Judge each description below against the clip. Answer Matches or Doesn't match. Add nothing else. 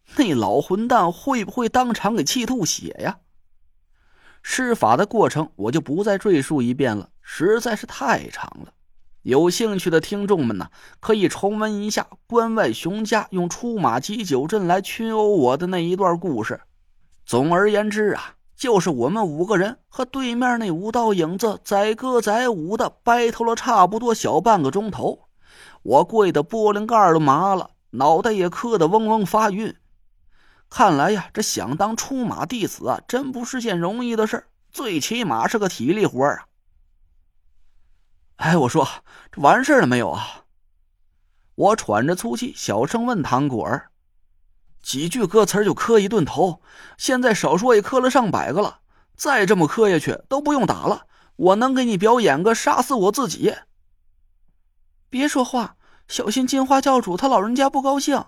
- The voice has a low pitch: Doesn't match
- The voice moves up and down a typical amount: Doesn't match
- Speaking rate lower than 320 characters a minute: Matches